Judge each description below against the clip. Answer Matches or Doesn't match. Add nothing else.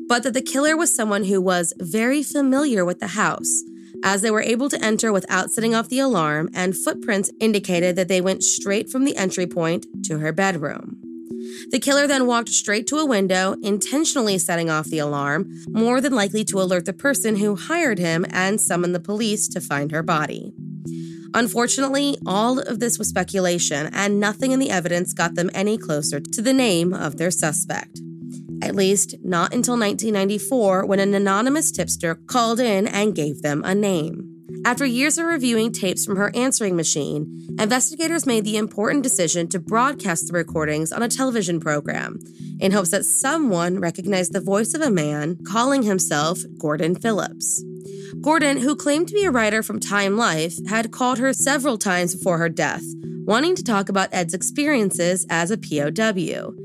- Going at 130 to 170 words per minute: Doesn't match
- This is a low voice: Doesn't match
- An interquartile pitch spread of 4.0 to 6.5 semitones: Matches